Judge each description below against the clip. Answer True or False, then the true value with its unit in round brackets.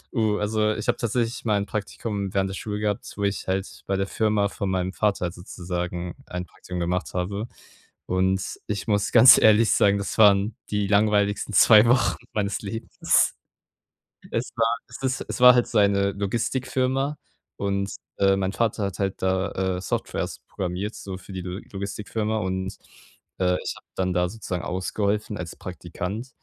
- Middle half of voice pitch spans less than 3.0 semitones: True (2.4 semitones)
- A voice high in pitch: False (100 Hz)